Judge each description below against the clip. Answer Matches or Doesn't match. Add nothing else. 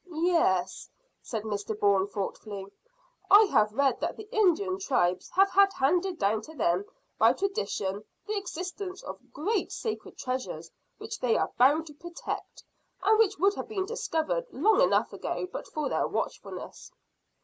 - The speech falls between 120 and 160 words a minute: Matches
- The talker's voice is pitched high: Matches